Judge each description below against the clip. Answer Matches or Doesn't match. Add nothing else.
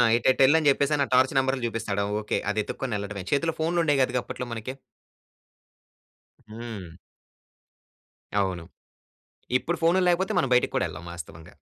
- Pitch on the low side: Matches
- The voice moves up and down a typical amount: Doesn't match